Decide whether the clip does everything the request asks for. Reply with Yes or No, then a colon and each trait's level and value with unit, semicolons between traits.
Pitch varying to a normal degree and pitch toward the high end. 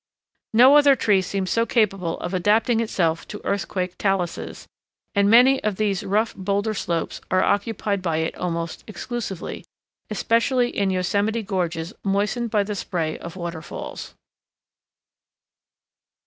Yes: average, 3.6 semitones; high, 200 Hz